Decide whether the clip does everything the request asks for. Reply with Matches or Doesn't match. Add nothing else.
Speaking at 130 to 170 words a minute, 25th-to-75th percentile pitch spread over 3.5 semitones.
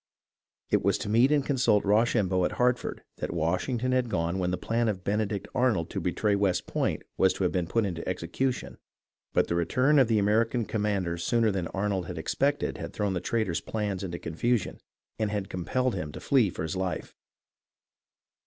Doesn't match